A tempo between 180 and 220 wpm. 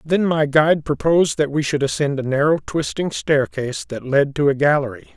Yes: average, 200 wpm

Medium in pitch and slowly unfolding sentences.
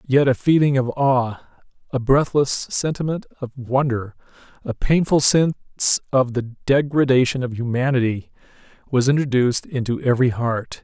No: low, 130 Hz; slow, 125 wpm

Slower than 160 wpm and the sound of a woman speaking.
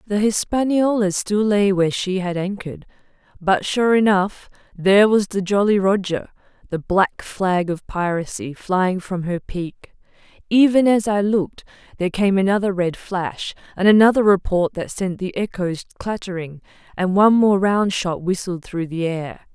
Yes: average, 150 wpm; female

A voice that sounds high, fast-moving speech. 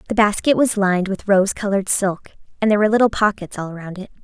Yes: high, 200 Hz; fast, 225 wpm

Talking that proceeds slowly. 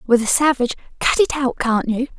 No: fast, 220 wpm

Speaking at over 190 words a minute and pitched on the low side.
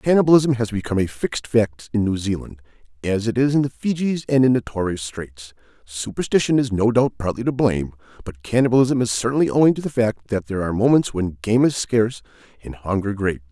Yes: average, 200 wpm; low, 115 Hz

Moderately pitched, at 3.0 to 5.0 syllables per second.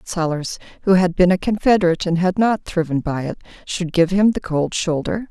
No: medium, 175 Hz; 5.3 syllables/s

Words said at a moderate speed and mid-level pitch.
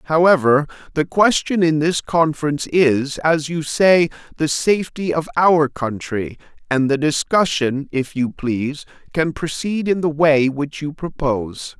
Yes: average, 150 wpm; medium, 150 Hz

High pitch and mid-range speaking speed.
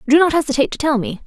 No: very high, 280 Hz; fast, 285 wpm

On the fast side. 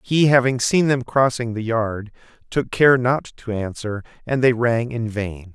No: average, 185 wpm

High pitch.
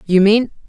Yes: high, 205 Hz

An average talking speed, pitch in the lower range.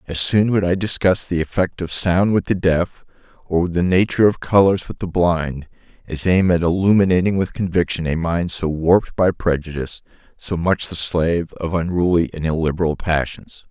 Yes: average, 180 wpm; very low, 90 Hz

